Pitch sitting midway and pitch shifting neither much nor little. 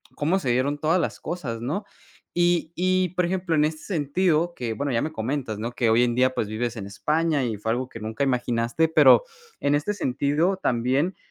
No: medium, 145 Hz; wide, 5.9 semitones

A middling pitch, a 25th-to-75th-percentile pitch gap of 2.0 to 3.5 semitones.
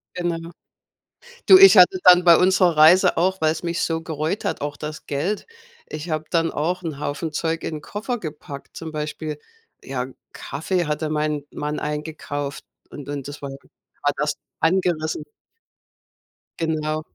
Yes: medium, 155 Hz; narrow, 2.6 semitones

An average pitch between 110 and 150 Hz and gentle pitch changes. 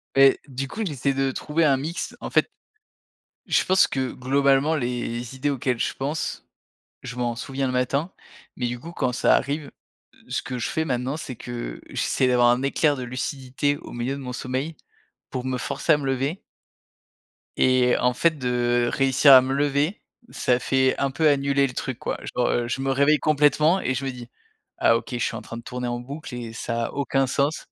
Yes: low, 135 Hz; narrow, 2.3 semitones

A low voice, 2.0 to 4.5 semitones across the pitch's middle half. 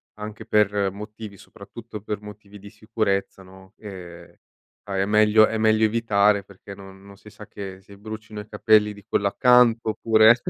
No: low, 105 Hz; narrow, 1.6 semitones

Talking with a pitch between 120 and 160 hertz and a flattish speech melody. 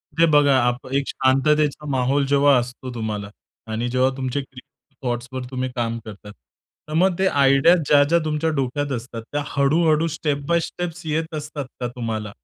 No: medium, 140 Hz; average, 3.4 semitones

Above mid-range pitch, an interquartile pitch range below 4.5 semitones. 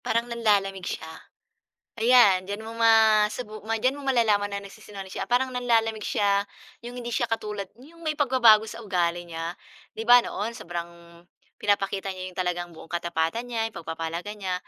Yes: high, 210 Hz; average, 4.1 semitones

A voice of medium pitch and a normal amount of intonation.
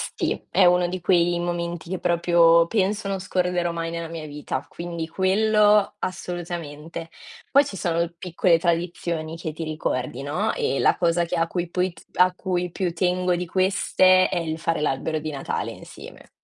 No: medium, 175 Hz; narrow, 1.8 semitones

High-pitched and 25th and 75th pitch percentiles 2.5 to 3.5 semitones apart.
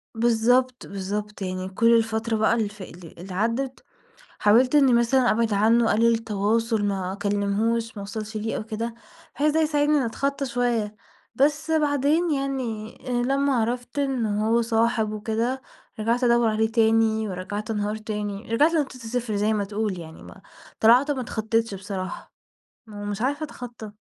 Yes: high, 225 Hz; average, 3.0 semitones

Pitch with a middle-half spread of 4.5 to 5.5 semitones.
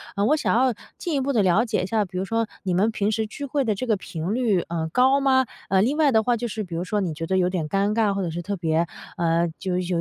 Yes: average, 4.9 semitones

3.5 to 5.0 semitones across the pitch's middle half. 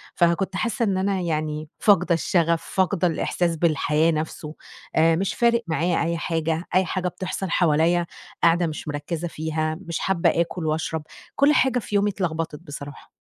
No: average, 2.9 semitones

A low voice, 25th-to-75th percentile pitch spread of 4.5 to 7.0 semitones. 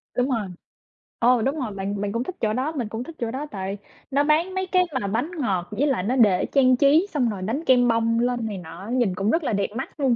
No: high, 245 Hz; average, 5.0 semitones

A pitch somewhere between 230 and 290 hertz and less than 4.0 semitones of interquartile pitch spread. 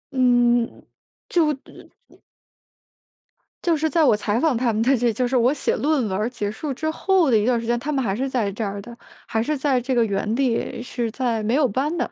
Yes: high, 245 Hz; average, 3.6 semitones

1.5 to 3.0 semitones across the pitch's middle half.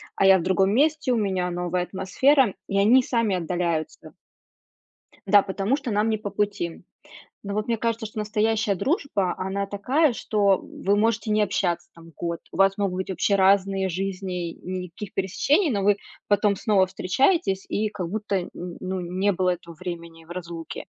Yes: average, 2.7 semitones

